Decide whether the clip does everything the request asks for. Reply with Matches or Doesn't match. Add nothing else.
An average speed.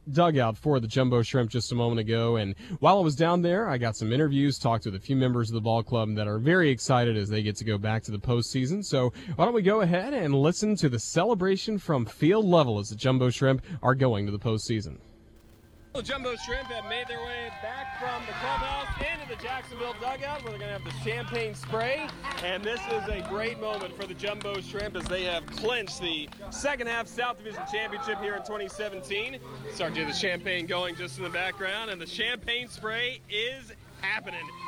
Doesn't match